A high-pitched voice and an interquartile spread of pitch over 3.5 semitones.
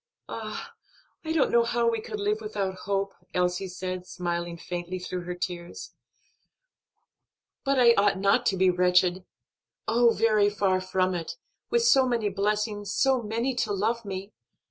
Yes: high, 200 Hz; average, 4.3 semitones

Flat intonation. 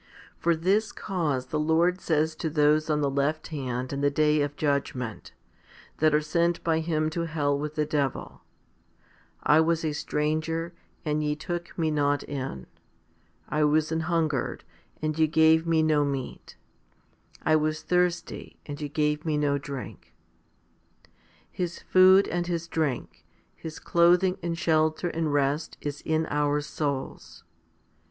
Yes: narrow, 2.1 semitones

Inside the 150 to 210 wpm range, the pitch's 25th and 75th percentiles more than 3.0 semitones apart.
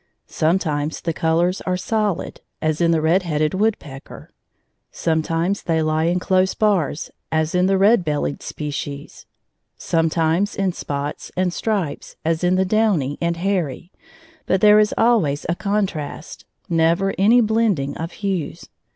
No: average, 140 wpm; average, 3.7 semitones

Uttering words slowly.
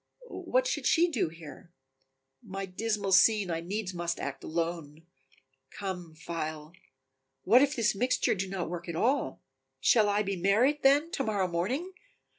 No: average, 155 wpm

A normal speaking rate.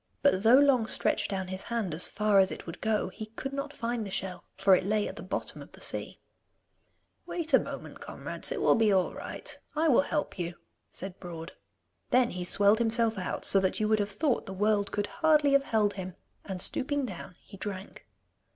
No: fast, 215 wpm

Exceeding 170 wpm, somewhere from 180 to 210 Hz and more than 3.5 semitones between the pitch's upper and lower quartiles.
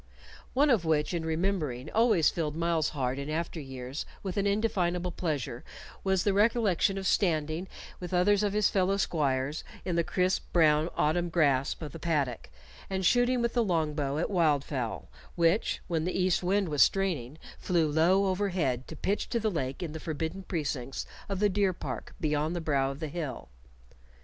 No: average, 180 wpm; medium, 170 Hz; average, 4.3 semitones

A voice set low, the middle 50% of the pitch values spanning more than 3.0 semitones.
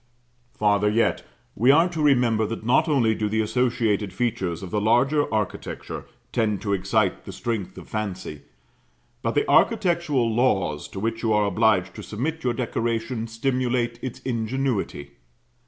Yes: low, 115 Hz; average, 3.4 semitones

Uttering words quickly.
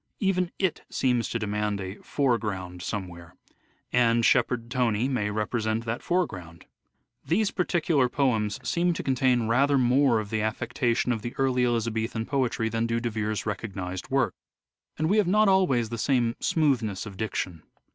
No: average, 160 wpm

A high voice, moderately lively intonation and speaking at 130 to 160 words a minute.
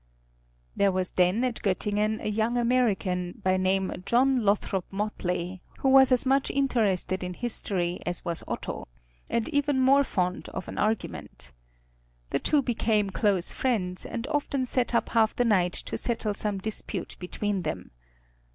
Yes: high, 210 Hz; average, 4.8 semitones; average, 155 wpm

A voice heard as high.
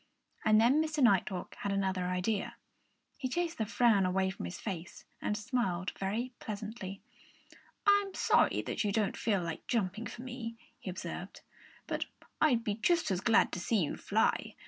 Yes: high, 210 Hz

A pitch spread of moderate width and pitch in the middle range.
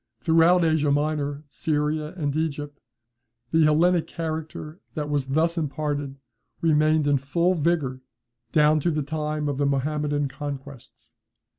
No: narrow, 1.8 semitones; medium, 150 Hz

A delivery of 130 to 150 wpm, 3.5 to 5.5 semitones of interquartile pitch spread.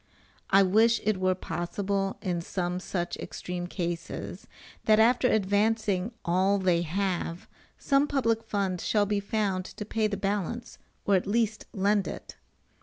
No: average, 145 wpm; average, 2.8 semitones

